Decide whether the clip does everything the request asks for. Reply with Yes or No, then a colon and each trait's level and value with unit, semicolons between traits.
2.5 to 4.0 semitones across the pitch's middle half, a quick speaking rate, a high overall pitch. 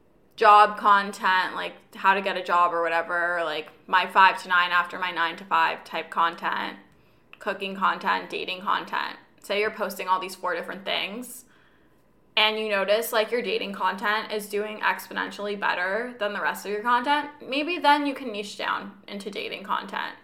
No: average, 2.8 semitones; average, 180 wpm; high, 205 Hz